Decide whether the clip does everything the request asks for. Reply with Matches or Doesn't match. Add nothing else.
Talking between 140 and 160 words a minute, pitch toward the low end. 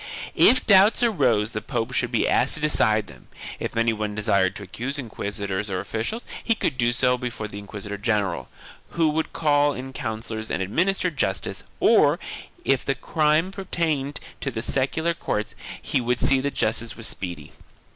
Doesn't match